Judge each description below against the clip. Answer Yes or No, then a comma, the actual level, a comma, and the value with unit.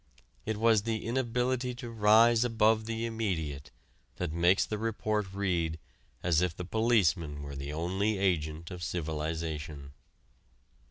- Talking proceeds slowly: Yes, slow, 130 wpm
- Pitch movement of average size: No, wide, 5.8 semitones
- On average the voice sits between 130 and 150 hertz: No, very low, 95 Hz